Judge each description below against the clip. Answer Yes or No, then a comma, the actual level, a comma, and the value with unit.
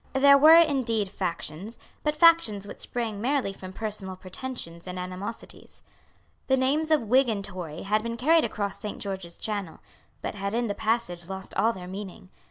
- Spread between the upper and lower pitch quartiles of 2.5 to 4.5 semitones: No, wide, 5.4 semitones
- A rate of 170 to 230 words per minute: Yes, average, 175 wpm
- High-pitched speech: Yes, high, 210 Hz